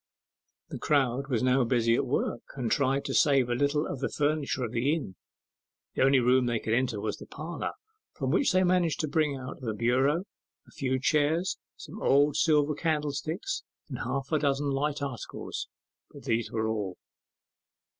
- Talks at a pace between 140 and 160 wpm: No, average, 180 wpm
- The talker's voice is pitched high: No, low, 135 Hz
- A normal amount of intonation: Yes, average, 3.4 semitones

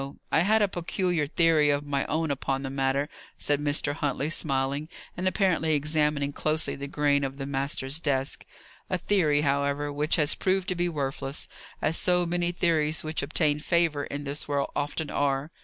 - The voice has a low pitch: No, medium, 150 Hz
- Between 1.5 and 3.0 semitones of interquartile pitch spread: Yes, average, 2.7 semitones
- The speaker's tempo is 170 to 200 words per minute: Yes, average, 175 wpm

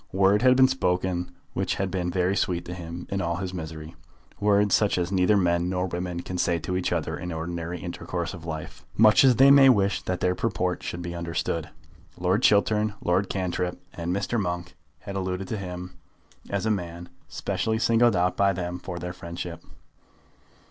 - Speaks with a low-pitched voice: Yes, very low, 90 Hz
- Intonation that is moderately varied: No, narrow, 2.3 semitones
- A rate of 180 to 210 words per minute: Yes, average, 190 wpm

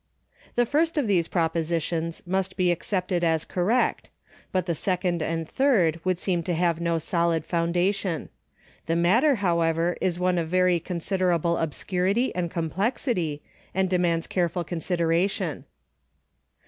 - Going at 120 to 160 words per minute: Yes, slow, 135 wpm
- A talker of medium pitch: Yes, medium, 175 Hz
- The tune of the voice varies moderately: No, narrow, 2.1 semitones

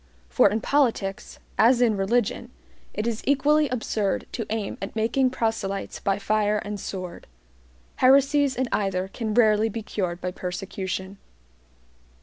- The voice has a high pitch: Yes, high, 215 Hz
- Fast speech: No, slow, 135 wpm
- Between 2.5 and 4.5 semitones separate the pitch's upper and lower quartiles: Yes, average, 3.8 semitones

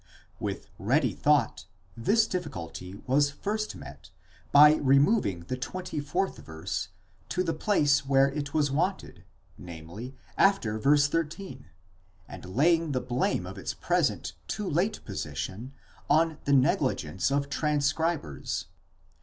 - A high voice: No, medium, 145 Hz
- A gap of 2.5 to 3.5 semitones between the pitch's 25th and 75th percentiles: No, wide, 5.4 semitones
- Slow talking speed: Yes, slow, 125 wpm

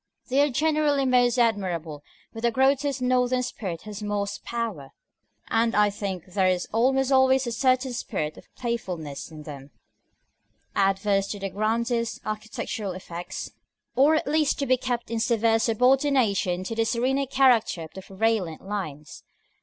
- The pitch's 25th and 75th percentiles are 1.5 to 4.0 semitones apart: No, average, 4.9 semitones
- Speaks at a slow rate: No, average, 155 wpm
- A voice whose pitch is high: Yes, high, 225 Hz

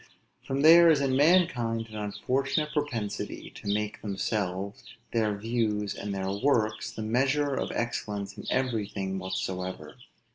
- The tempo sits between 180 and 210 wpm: No, slow, 135 wpm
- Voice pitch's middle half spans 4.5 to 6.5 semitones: Yes, average, 4.9 semitones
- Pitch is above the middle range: No, low, 110 Hz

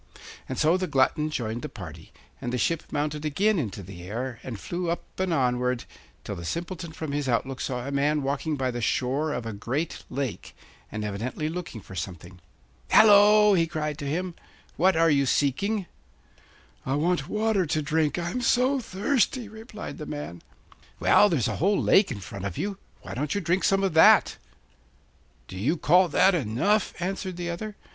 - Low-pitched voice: No, medium, 150 Hz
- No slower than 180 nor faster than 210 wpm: Yes, average, 185 wpm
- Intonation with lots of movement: Yes, wide, 6.8 semitones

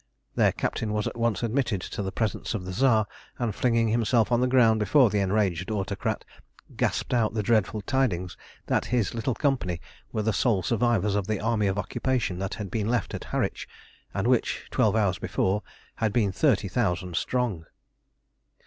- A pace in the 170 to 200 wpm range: Yes, average, 180 wpm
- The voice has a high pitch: No, low, 110 Hz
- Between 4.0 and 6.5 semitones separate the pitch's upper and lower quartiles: No, average, 3.3 semitones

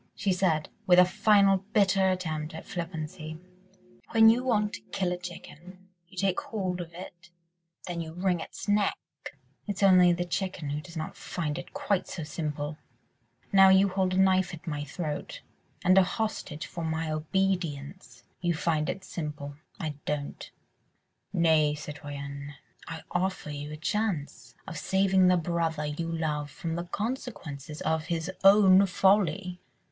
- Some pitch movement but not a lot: Yes, average, 3.7 semitones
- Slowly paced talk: No, average, 155 wpm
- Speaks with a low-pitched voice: No, medium, 175 Hz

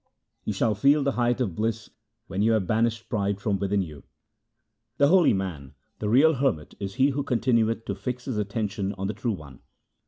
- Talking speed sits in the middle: Yes, average, 195 wpm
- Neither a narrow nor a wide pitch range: Yes, average, 4.2 semitones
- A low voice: Yes, low, 110 Hz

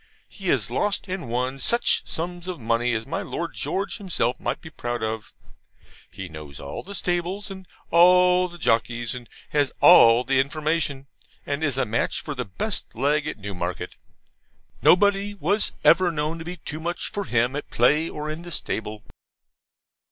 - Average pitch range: No, wide, 6.8 semitones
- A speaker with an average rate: Yes, average, 175 wpm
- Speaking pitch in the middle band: Yes, medium, 150 Hz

